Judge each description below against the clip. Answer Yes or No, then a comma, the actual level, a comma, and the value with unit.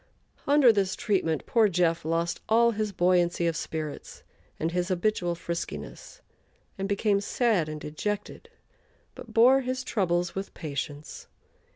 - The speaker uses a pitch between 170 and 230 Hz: Yes, medium, 185 Hz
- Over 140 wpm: No, slow, 135 wpm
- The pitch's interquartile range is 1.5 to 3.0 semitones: No, average, 4.5 semitones